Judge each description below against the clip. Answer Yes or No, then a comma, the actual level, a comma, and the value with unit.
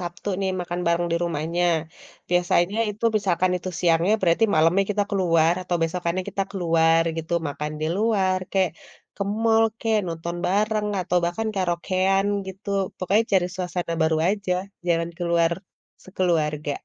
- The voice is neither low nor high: Yes, medium, 175 Hz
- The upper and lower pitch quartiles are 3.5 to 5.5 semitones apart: No, narrow, 2.5 semitones